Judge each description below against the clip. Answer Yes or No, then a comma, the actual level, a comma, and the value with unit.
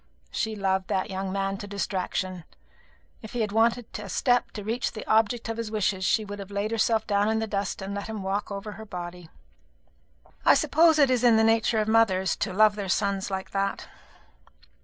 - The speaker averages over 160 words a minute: Yes, fast, 205 wpm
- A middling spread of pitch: No, narrow, 2.2 semitones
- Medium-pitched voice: No, high, 205 Hz